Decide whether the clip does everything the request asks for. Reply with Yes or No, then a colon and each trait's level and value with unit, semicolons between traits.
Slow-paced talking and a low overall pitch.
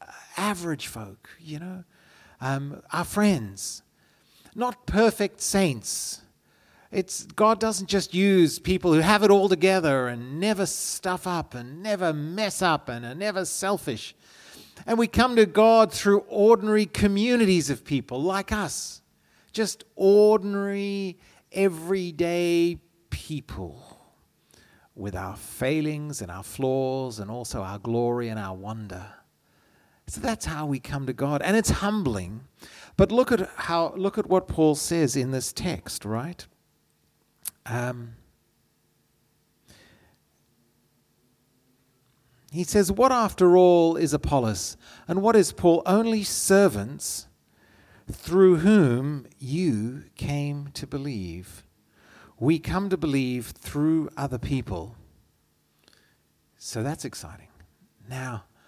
No: slow, 120 wpm; medium, 155 Hz